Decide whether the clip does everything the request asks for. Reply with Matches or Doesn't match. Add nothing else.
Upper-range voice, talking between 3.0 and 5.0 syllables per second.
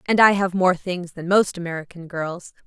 Doesn't match